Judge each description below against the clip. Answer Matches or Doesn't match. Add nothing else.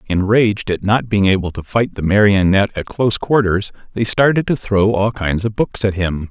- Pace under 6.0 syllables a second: Matches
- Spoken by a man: Matches